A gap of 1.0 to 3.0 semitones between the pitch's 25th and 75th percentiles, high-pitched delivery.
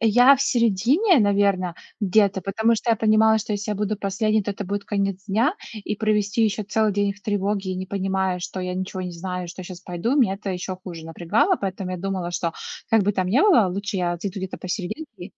Yes: narrow, 2.6 semitones; high, 200 Hz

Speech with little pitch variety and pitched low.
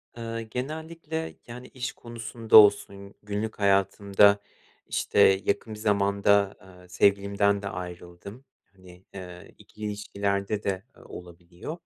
Yes: narrow, 2.3 semitones; low, 100 Hz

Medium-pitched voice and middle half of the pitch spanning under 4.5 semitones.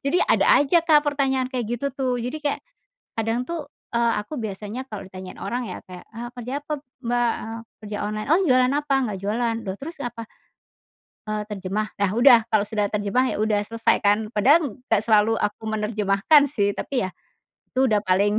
No: high, 230 Hz; average, 4.0 semitones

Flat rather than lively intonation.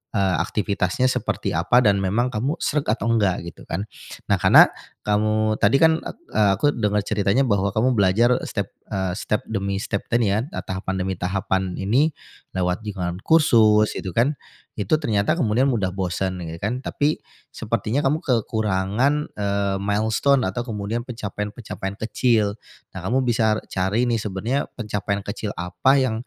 No: average, 3.7 semitones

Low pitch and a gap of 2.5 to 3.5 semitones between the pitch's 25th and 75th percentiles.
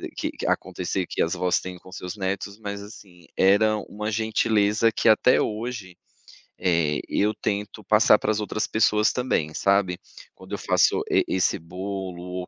Yes: low, 100 Hz; average, 2.8 semitones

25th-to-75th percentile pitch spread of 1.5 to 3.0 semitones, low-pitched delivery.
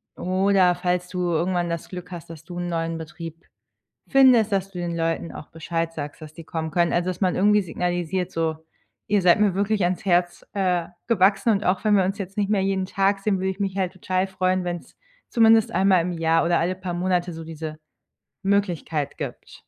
No: narrow, 2.6 semitones; medium, 180 Hz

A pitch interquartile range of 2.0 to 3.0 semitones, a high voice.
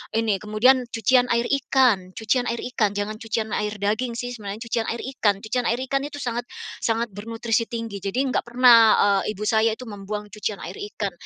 Yes: narrow, 2.5 semitones; high, 225 Hz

